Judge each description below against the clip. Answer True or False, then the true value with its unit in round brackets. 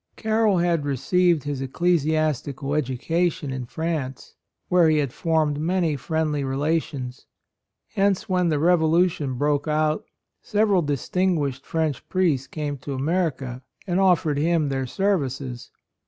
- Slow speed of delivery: True (125 wpm)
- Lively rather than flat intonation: False (4.0 semitones)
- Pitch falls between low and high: True (155 Hz)